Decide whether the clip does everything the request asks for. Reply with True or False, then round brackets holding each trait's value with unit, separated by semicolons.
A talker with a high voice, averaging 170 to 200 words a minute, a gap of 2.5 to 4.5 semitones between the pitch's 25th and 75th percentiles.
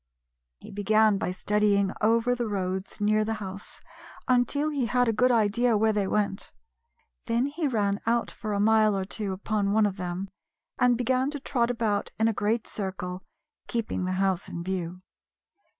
True (215 Hz; 175 wpm; 3.1 semitones)